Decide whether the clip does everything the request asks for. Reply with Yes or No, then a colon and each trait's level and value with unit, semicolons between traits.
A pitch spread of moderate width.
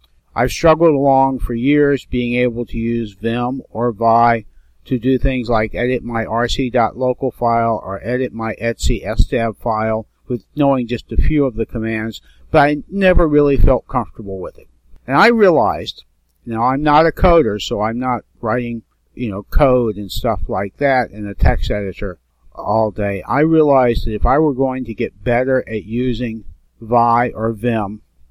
Yes: average, 3.1 semitones